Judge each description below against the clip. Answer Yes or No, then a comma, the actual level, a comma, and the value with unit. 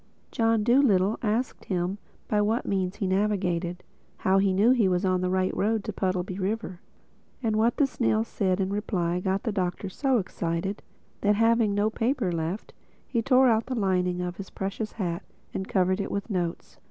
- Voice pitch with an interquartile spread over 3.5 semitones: No, average, 3.2 semitones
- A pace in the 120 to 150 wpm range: No, average, 180 wpm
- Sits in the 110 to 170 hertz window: No, high, 195 Hz